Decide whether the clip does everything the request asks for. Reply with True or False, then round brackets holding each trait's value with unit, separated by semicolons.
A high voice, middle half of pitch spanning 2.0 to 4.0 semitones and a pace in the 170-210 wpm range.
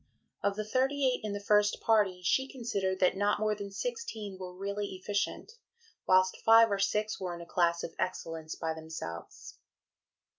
True (200 Hz; 2.9 semitones; 175 wpm)